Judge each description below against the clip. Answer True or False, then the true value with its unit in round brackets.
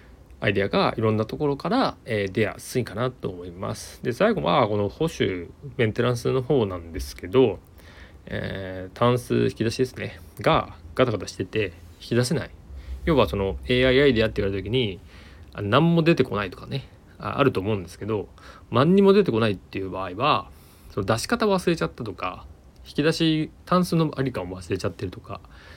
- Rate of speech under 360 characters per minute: False (370 characters per minute)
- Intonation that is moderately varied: False (5.8 semitones)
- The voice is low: True (105 Hz)